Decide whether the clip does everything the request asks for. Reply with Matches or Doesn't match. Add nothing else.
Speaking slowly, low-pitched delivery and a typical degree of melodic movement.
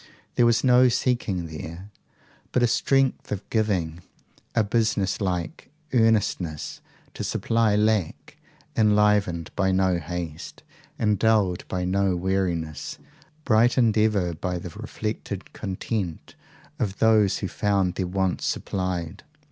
Matches